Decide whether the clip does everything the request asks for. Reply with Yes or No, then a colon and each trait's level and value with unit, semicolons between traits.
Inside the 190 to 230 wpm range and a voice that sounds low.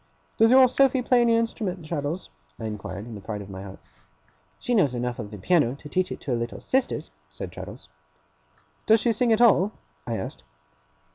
No: fast, 205 wpm; medium, 165 Hz